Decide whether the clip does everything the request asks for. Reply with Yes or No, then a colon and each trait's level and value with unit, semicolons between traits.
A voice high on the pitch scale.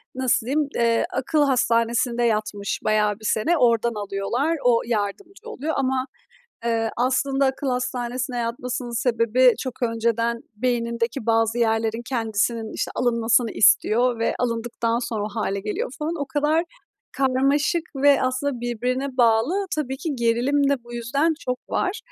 Yes: high, 240 Hz